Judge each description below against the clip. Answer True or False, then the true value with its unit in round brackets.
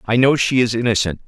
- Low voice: True (115 Hz)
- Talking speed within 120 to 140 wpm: False (235 wpm)